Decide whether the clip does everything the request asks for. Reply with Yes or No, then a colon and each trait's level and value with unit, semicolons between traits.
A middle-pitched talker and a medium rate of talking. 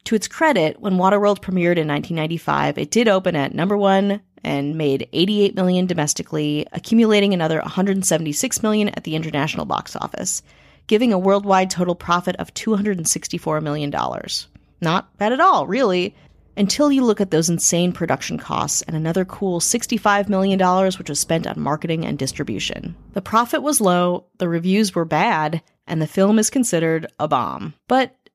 Yes: medium, 180 Hz; average, 165 wpm